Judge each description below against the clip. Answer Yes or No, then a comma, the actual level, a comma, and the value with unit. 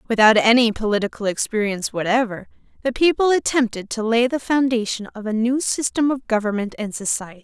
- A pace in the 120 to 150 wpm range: No, average, 160 wpm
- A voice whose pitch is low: No, high, 230 Hz